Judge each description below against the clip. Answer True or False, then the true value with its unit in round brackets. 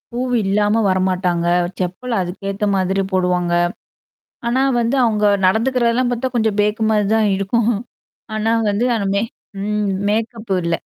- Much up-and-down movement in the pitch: False (3.2 semitones)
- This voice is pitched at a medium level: False (210 Hz)